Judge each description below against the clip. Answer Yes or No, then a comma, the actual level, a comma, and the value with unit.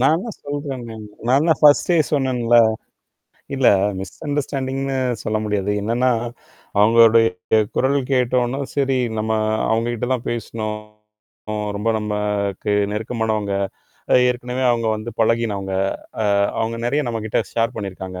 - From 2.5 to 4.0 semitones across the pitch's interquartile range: Yes, average, 3.4 semitones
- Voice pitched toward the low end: Yes, low, 115 Hz